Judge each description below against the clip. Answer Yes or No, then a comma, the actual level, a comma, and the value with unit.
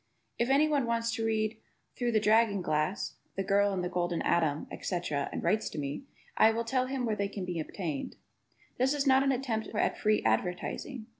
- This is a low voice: No, high, 215 Hz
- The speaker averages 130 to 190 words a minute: No, average, 200 wpm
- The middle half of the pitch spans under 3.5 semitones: No, average, 5.1 semitones